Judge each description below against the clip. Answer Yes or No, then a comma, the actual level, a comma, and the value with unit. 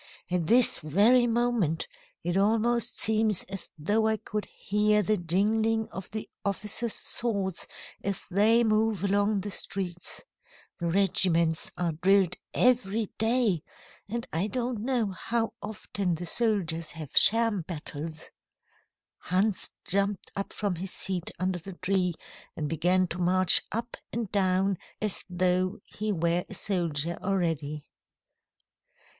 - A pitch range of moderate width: Yes, average, 3.6 semitones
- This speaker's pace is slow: Yes, slow, 130 wpm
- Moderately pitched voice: No, high, 195 Hz